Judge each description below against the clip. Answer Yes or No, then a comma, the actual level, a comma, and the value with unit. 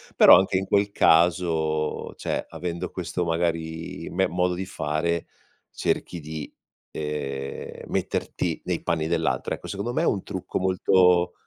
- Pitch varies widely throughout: No, narrow, 2.6 semitones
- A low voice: Yes, very low, 85 Hz